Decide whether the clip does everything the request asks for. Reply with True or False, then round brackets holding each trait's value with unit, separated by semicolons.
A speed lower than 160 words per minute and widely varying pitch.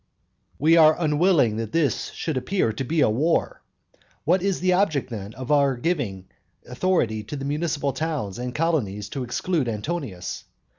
False (165 wpm; 6.3 semitones)